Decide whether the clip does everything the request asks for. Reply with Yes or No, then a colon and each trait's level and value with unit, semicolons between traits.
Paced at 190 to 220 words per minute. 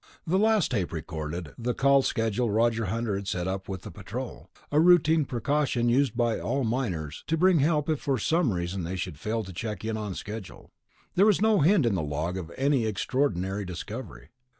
Yes: average, 195 wpm